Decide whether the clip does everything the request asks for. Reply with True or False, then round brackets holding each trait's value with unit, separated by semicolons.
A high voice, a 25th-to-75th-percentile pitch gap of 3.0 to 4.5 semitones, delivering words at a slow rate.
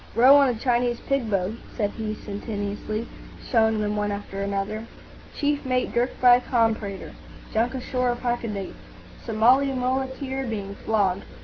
True (230 Hz; 3.5 semitones; 130 wpm)